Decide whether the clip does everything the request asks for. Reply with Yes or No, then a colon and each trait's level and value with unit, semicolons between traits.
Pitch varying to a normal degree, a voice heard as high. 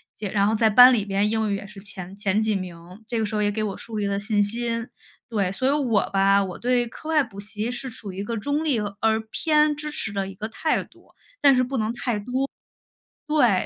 Yes: average, 3.2 semitones; high, 215 Hz